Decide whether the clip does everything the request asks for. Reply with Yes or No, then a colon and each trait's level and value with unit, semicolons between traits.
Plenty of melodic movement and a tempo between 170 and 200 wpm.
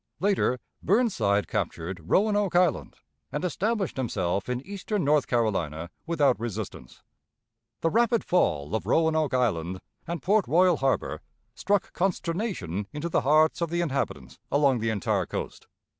No: wide, 8.8 semitones; slow, 135 wpm